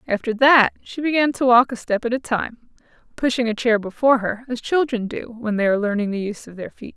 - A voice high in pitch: Yes, high, 235 Hz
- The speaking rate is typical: No, fast, 240 wpm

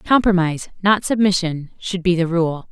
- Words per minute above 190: No, average, 155 wpm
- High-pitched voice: No, medium, 180 Hz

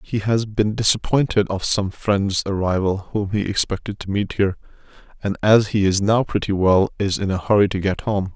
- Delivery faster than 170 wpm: Yes, average, 200 wpm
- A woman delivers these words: No, male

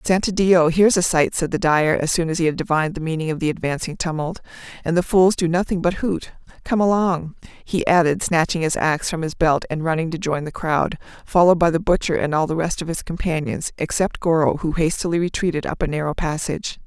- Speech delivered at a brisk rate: Yes, fast, 220 wpm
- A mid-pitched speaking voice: Yes, medium, 165 Hz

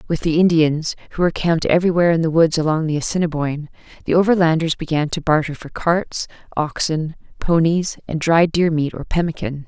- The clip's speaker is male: No, female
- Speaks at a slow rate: No, average, 175 wpm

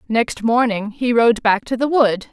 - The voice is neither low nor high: No, high, 230 Hz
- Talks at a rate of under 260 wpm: Yes, fast, 205 wpm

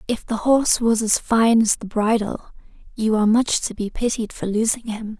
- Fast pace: Yes, fast, 210 wpm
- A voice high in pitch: Yes, high, 220 Hz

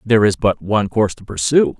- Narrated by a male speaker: Yes, male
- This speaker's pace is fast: Yes, fast, 235 wpm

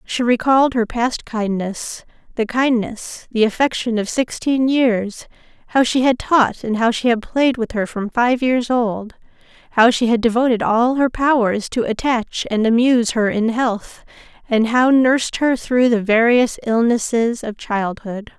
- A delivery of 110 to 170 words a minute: Yes, average, 155 wpm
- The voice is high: Yes, high, 235 Hz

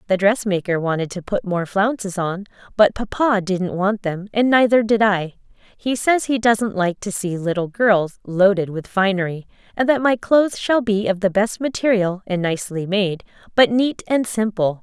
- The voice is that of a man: No, female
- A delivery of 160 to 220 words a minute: Yes, average, 185 wpm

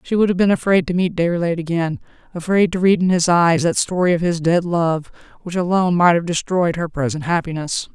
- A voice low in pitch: No, medium, 170 Hz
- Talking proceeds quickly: Yes, fast, 220 wpm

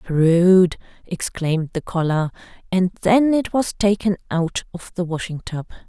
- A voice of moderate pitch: Yes, medium, 180 Hz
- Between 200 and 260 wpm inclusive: No, average, 145 wpm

